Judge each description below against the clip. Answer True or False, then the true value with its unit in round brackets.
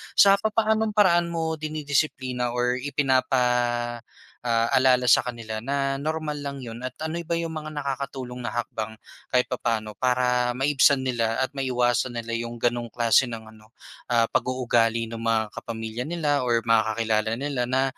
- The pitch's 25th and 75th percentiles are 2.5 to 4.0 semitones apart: True (3.3 semitones)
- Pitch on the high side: False (125 Hz)